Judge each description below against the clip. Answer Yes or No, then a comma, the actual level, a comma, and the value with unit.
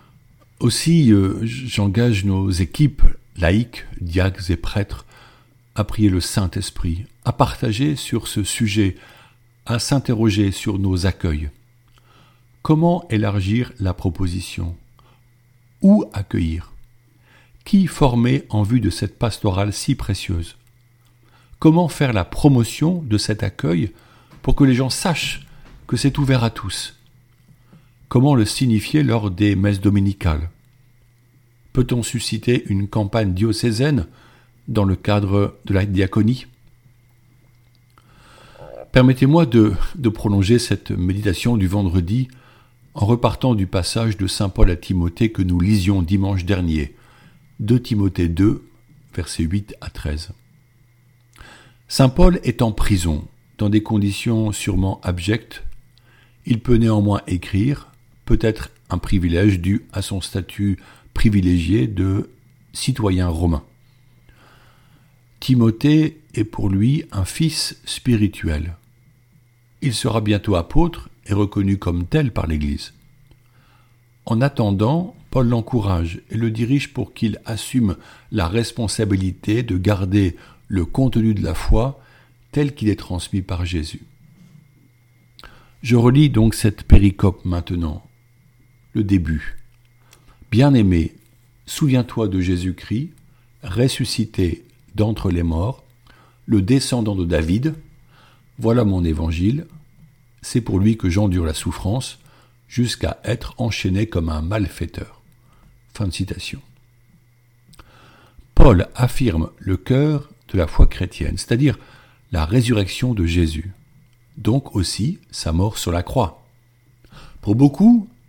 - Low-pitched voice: Yes, low, 115 Hz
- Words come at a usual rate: No, slow, 115 wpm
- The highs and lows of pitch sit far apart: No, average, 4.2 semitones